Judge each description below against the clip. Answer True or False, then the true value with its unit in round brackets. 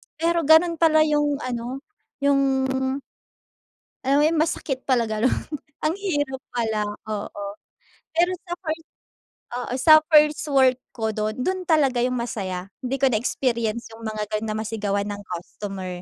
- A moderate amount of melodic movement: False (5.9 semitones)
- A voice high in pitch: True (255 Hz)